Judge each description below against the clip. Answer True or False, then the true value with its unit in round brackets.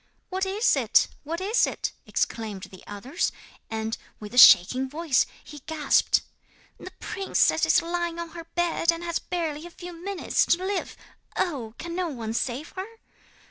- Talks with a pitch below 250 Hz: False (335 Hz)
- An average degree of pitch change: False (5.7 semitones)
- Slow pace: False (165 wpm)